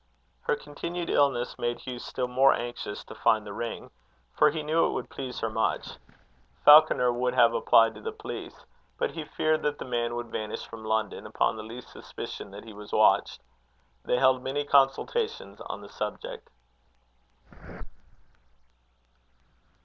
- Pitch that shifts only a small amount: No, average, 4.3 semitones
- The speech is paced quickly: No, average, 155 wpm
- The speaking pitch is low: Yes, low, 125 Hz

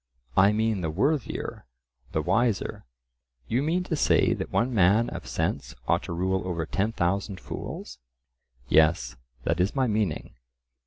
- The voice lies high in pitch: No, low, 100 Hz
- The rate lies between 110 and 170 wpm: Yes, average, 150 wpm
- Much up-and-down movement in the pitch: No, average, 4.9 semitones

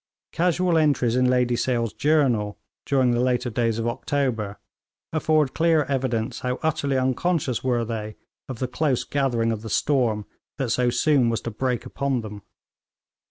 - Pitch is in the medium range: No, low, 125 Hz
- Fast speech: No, average, 160 wpm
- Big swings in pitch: No, average, 3.3 semitones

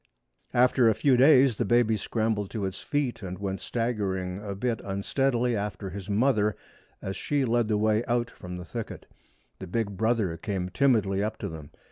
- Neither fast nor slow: Yes, average, 180 wpm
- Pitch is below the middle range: Yes, low, 110 Hz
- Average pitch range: Yes, average, 3.7 semitones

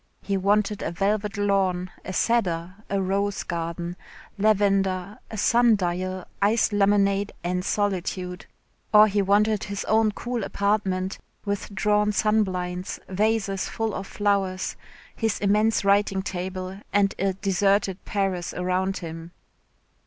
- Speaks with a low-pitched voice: No, high, 195 Hz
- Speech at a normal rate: No, slow, 125 wpm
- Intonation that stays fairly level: Yes, narrow, 2.0 semitones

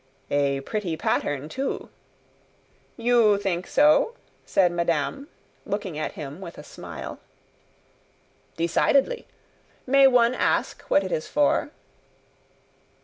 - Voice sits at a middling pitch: No, high, 195 Hz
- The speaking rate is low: Yes, slow, 105 wpm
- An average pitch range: No, wide, 7.9 semitones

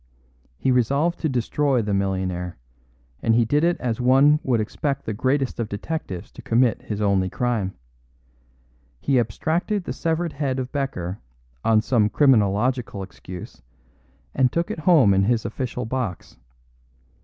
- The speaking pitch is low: Yes, low, 125 Hz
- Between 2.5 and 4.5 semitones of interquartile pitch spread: No, average, 5.1 semitones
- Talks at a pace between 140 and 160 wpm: Yes, average, 145 wpm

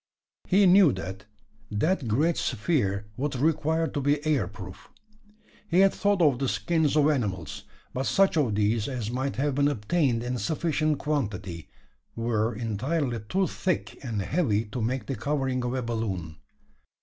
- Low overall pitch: Yes, low, 130 Hz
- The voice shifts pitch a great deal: Yes, wide, 6.0 semitones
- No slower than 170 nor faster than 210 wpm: No, average, 160 wpm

